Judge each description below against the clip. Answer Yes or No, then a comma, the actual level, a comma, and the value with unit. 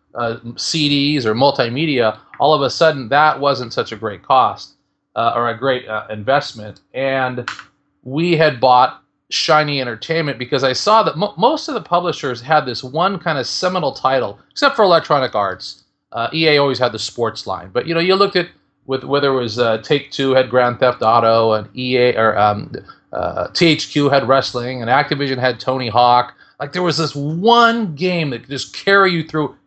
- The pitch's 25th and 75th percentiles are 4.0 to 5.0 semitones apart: Yes, average, 4.3 semitones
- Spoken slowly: No, average, 190 wpm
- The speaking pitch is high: No, low, 135 Hz